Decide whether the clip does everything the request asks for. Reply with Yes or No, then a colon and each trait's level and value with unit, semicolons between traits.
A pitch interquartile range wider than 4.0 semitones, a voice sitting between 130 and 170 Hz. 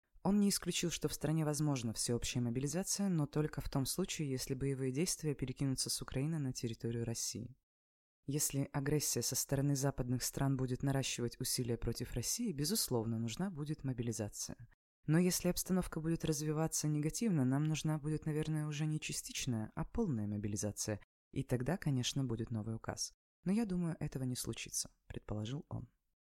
Yes: average, 4.7 semitones; low, 135 Hz